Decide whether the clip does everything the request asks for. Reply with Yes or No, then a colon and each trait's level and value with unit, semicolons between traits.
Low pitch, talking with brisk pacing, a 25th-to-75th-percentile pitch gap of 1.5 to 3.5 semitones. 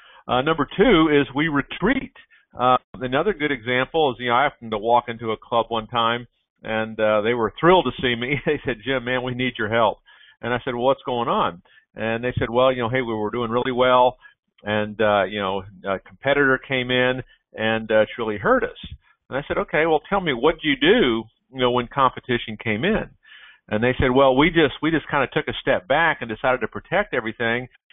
Yes: low, 125 Hz; fast, 230 wpm; average, 3.0 semitones